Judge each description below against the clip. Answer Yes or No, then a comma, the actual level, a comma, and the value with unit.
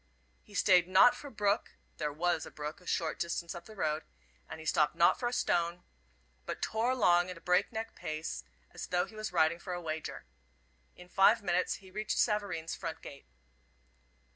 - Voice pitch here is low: No, medium, 175 Hz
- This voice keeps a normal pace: Yes, average, 190 wpm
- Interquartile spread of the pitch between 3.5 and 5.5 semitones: Yes, average, 4.1 semitones